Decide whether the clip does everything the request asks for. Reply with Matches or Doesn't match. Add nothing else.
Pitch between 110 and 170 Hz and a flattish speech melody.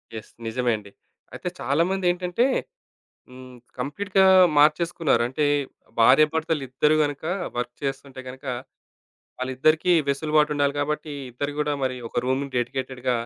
Doesn't match